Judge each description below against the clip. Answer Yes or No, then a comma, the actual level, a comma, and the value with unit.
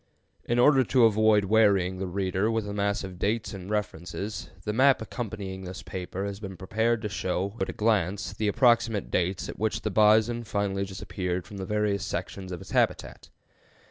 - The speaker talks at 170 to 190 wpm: Yes, average, 185 wpm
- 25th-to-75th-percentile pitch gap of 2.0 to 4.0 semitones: Yes, narrow, 2.5 semitones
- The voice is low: Yes, low, 100 Hz